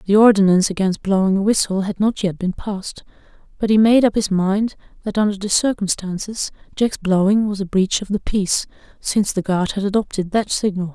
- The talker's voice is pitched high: Yes, high, 200 Hz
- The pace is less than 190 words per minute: No, average, 195 wpm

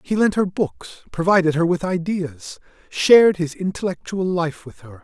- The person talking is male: Yes, male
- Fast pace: No, average, 165 wpm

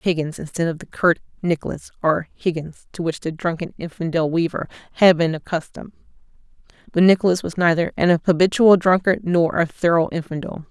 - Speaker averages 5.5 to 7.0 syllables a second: Yes, 5.6 syllables/s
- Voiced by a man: No, female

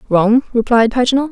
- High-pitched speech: Yes, high, 240 Hz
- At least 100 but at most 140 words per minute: Yes, slow, 135 wpm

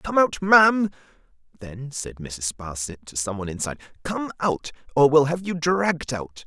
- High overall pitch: No, medium, 140 Hz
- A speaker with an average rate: Yes, average, 175 wpm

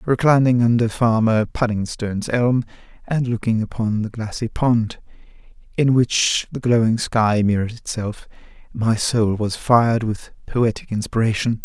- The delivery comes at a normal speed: No, slow, 130 wpm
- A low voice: Yes, low, 115 Hz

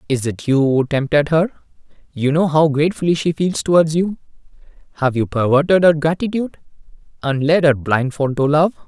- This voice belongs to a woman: No, male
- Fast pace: No, average, 160 wpm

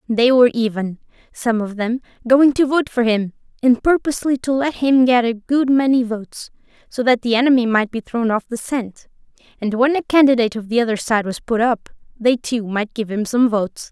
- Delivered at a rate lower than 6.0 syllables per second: Yes, 5.4 syllables/s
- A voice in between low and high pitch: No, high, 240 Hz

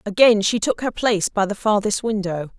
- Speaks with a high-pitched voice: Yes, high, 210 Hz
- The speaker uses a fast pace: Yes, fast, 210 wpm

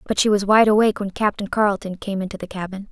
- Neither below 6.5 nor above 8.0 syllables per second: Yes, 6.8 syllables/s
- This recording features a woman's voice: Yes, female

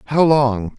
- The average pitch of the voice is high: No, low, 130 Hz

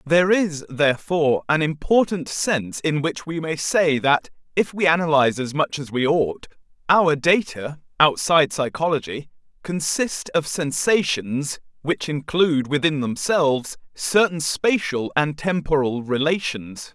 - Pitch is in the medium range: Yes, medium, 155 Hz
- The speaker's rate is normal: No, slow, 125 wpm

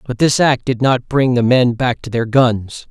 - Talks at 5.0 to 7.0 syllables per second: No, 4.3 syllables/s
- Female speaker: No, male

